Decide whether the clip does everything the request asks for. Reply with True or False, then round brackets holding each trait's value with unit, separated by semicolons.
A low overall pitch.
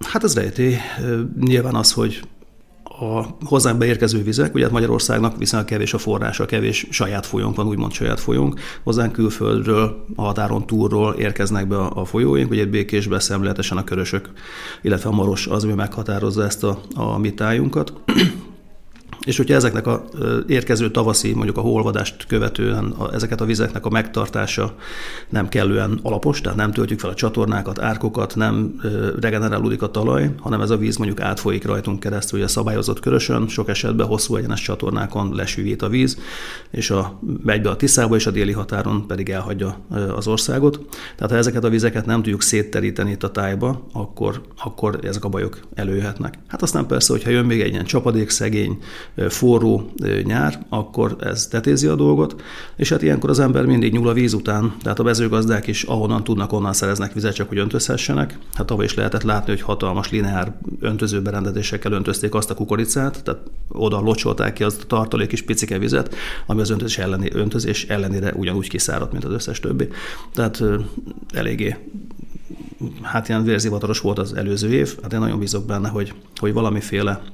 True (105 Hz)